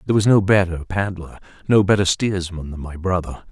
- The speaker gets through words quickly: No, average, 190 wpm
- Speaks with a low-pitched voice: Yes, very low, 90 Hz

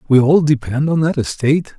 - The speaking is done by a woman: No, male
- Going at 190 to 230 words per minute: Yes, average, 200 wpm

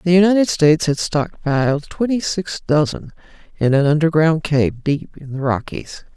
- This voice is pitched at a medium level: Yes, medium, 155 Hz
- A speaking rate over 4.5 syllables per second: Yes, 4.7 syllables/s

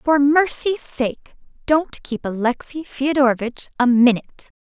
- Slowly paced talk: Yes, slow, 115 wpm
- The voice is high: Yes, very high, 270 Hz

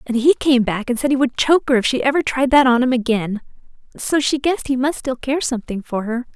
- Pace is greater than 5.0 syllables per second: Yes, 6.0 syllables/s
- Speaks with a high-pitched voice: Yes, very high, 255 Hz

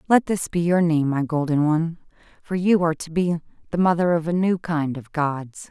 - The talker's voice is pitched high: No, medium, 165 Hz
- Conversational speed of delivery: No, fast, 220 wpm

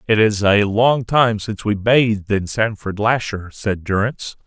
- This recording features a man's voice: Yes, male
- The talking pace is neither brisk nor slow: Yes, average, 175 wpm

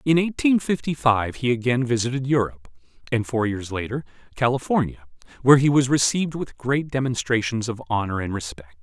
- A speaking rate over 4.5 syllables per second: Yes, 5.7 syllables/s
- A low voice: Yes, low, 125 Hz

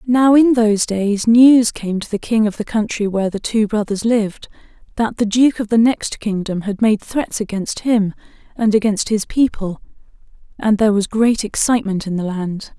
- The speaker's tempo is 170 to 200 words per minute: Yes, average, 190 wpm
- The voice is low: No, high, 215 Hz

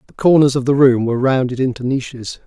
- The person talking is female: No, male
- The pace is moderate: No, fast, 220 wpm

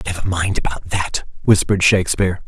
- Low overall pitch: Yes, very low, 90 Hz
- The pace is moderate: Yes, average, 145 wpm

